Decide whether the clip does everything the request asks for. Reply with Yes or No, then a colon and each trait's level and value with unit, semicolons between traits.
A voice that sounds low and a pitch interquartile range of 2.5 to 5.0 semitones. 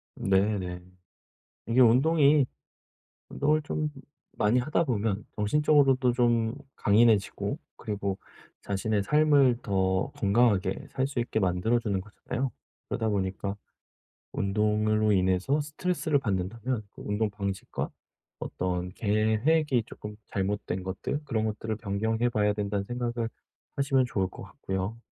Yes: low, 110 Hz; average, 4.1 semitones